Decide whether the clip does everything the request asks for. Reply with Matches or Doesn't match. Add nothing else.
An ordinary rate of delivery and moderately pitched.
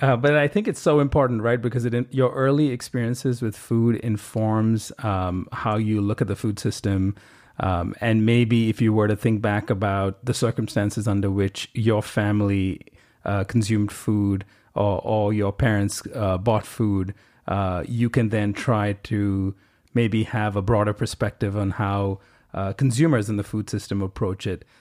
Doesn't match